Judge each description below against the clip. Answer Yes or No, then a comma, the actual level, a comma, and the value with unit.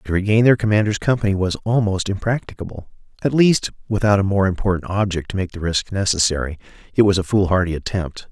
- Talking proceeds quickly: No, average, 180 wpm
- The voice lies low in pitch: Yes, low, 100 Hz